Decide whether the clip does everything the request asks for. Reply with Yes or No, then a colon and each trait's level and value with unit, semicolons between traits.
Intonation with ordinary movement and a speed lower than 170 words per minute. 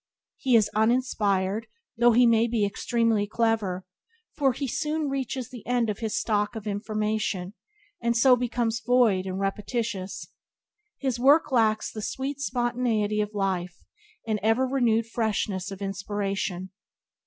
Yes: average, 3.1 semitones; average, 140 wpm